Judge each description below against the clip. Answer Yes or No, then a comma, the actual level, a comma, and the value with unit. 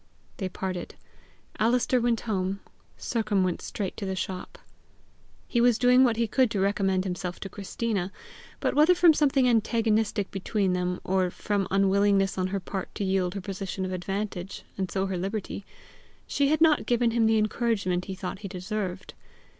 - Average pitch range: Yes, average, 3.5 semitones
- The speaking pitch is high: Yes, high, 200 Hz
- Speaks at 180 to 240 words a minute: No, average, 170 wpm